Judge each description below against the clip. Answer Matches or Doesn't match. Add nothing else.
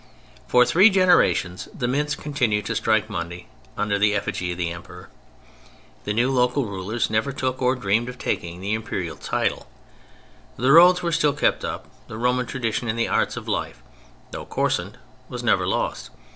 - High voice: Doesn't match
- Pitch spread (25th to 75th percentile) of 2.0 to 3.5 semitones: Doesn't match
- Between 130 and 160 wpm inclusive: Doesn't match